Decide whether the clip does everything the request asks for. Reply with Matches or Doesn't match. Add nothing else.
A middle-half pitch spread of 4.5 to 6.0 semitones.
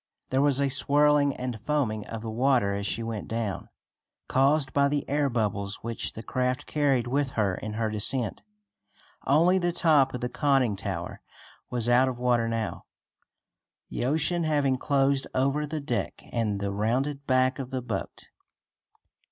Doesn't match